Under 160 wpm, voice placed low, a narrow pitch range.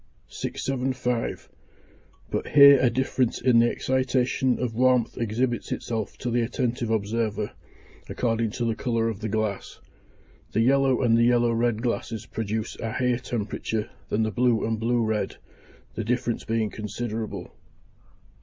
Yes: average, 145 wpm; low, 115 Hz; narrow, 1.9 semitones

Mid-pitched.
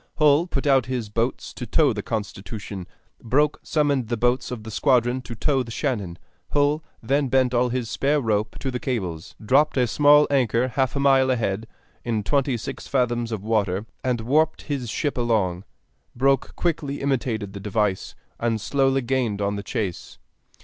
No: low, 125 Hz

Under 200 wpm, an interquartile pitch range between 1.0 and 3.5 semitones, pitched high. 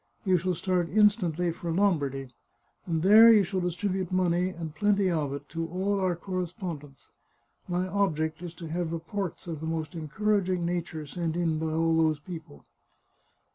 No: average, 175 wpm; narrow, 2.6 semitones; medium, 175 Hz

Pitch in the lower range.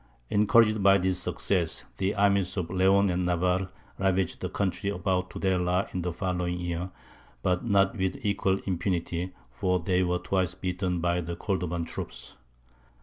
Yes: very low, 90 Hz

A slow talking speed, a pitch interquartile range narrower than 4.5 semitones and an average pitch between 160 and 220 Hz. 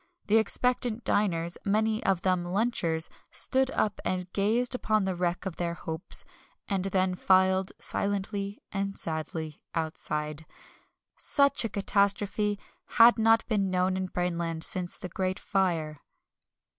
Yes: slow, 130 wpm; average, 3.2 semitones; high, 190 Hz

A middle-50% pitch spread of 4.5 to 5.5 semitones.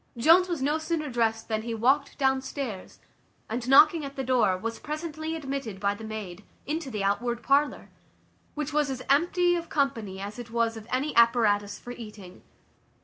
Yes: average, 5.2 semitones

